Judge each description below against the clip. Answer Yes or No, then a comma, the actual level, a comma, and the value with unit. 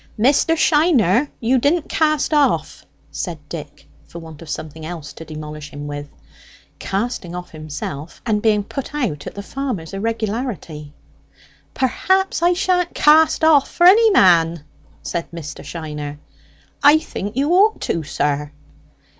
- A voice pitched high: Yes, high, 200 Hz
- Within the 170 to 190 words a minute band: No, average, 140 wpm